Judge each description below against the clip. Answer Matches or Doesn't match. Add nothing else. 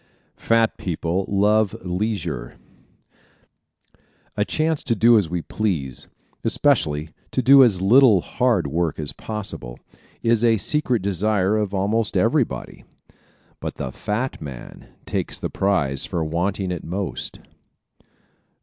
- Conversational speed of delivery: Doesn't match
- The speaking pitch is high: Doesn't match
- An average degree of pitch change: Matches